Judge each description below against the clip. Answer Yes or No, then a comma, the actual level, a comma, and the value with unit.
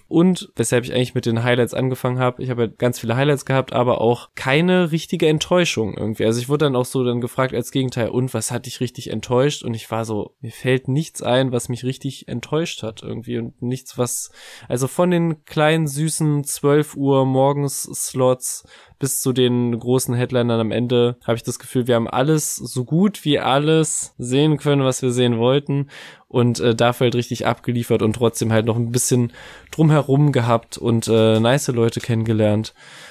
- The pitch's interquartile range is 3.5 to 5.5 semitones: No, average, 3.0 semitones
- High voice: No, low, 125 Hz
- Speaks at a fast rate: Yes, fast, 195 wpm